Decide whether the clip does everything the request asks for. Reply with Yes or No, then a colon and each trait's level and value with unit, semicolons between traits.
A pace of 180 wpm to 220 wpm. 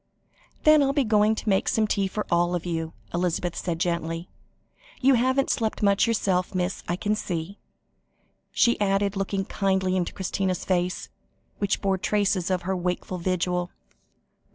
No: average, 155 wpm